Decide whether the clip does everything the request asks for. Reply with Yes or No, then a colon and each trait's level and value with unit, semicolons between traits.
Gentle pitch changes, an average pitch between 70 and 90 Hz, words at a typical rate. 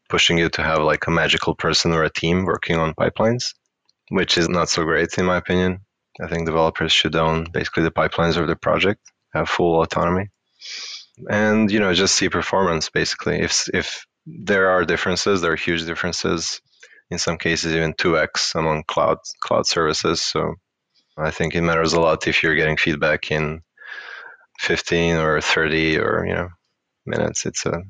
Yes: narrow, 1.7 semitones; very low, 85 Hz; average, 180 wpm